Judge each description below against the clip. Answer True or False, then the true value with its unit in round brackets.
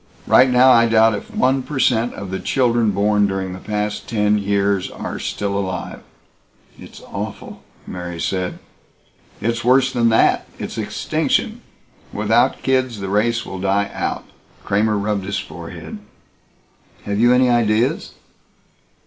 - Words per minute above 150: False (140 wpm)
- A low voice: True (105 Hz)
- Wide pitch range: False (3.1 semitones)